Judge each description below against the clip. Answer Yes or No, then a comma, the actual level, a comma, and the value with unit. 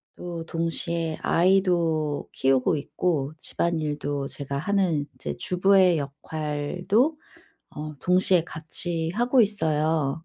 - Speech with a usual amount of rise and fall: Yes, average, 3.4 semitones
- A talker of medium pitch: Yes, medium, 165 Hz